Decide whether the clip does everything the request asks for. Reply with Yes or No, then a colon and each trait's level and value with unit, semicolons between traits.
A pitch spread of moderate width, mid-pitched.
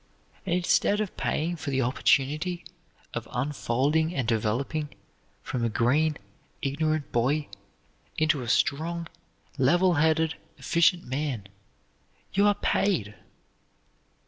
Yes: average, 4.6 semitones; medium, 150 Hz